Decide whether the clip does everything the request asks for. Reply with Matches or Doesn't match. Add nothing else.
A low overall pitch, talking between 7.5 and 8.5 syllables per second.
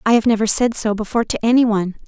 Doesn't match